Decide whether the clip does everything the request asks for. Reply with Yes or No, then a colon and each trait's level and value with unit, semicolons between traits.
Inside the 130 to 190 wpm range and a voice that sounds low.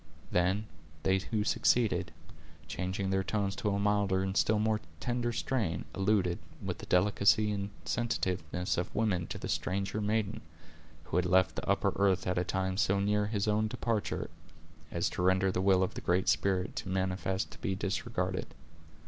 Yes: average, 175 wpm; low, 100 Hz